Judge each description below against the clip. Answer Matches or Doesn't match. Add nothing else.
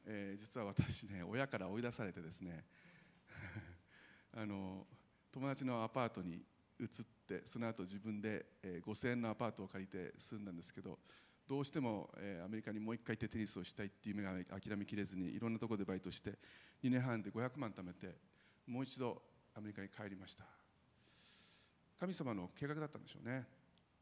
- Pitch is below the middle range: Matches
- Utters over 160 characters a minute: Matches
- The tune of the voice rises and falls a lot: Doesn't match